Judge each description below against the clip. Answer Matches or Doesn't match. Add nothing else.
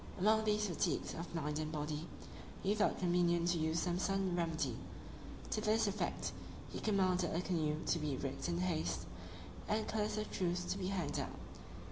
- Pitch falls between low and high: Matches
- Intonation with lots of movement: Doesn't match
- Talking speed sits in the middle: Matches